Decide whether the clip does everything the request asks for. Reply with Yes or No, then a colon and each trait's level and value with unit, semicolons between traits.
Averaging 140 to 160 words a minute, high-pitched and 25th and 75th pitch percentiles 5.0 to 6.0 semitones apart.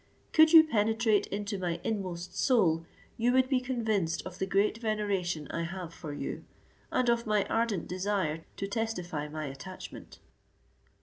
No: average, 150 wpm; high, 200 Hz; average, 4.6 semitones